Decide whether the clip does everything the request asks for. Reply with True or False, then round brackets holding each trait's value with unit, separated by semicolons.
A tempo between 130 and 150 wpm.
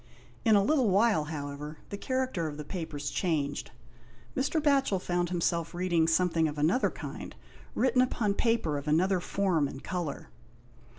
False (160 wpm)